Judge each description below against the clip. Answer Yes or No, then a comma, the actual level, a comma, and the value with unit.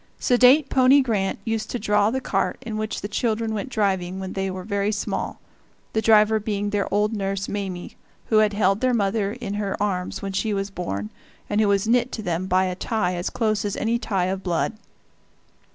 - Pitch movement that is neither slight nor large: No, narrow, 2.3 semitones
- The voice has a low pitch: No, high, 205 Hz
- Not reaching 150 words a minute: No, fast, 205 wpm